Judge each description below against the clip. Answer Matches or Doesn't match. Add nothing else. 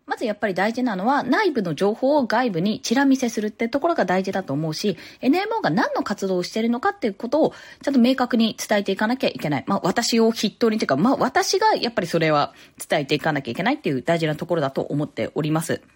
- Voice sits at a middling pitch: Doesn't match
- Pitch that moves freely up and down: Matches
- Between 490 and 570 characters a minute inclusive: Matches